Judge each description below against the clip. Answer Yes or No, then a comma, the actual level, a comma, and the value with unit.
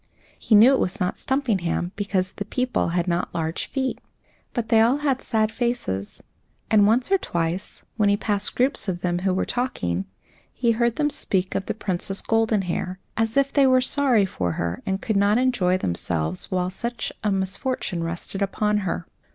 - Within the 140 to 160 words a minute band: No, average, 185 wpm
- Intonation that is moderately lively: Yes, average, 4.9 semitones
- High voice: Yes, high, 205 Hz